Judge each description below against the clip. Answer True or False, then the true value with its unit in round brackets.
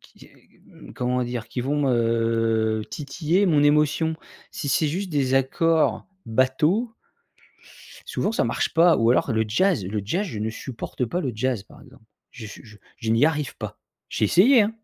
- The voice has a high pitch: False (135 Hz)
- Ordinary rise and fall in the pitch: False (6.4 semitones)